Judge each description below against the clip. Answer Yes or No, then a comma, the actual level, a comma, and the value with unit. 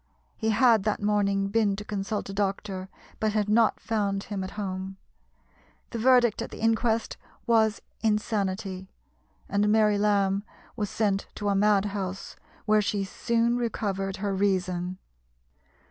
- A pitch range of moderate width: No, narrow, 1.9 semitones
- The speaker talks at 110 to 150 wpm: Yes, average, 145 wpm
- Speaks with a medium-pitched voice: No, high, 205 Hz